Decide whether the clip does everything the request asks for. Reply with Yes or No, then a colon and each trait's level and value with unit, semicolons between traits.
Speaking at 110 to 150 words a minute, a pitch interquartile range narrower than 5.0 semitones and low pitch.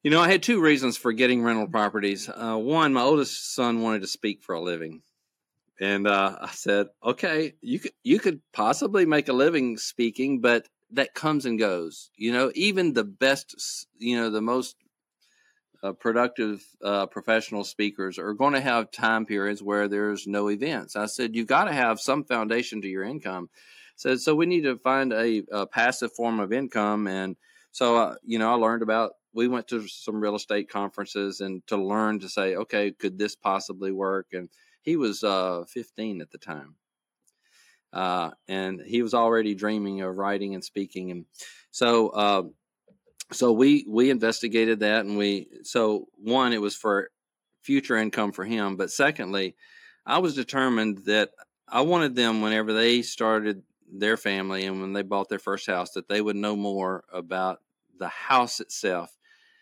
No: average, 180 wpm; average, 3.4 semitones; low, 110 Hz